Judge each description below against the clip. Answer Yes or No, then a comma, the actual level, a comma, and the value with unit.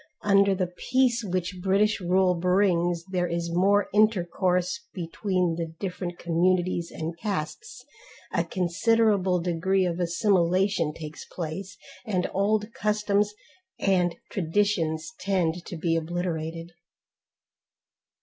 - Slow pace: Yes, slow, 110 wpm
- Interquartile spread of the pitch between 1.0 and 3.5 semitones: Yes, average, 2.8 semitones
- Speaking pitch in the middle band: Yes, medium, 180 Hz